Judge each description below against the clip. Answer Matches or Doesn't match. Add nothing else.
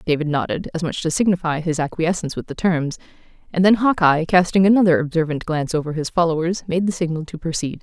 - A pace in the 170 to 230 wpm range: Matches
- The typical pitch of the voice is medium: Matches